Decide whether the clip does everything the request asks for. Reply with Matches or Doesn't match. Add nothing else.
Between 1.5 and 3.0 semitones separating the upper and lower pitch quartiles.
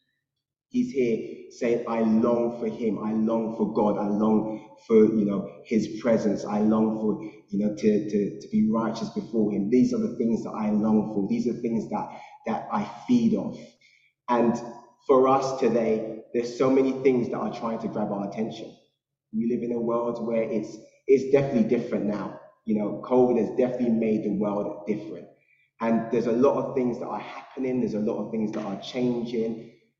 Matches